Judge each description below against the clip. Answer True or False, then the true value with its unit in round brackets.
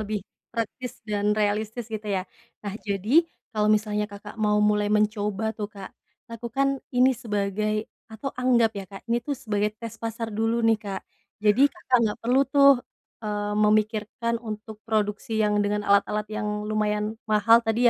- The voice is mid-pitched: False (215 Hz)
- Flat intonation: True (1.6 semitones)